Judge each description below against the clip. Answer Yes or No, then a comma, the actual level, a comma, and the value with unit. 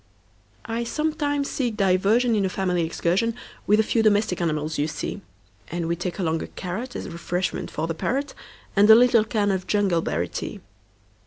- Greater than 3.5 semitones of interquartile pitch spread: Yes, average, 5.1 semitones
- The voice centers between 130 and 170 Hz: No, high, 200 Hz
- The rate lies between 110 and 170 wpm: Yes, average, 150 wpm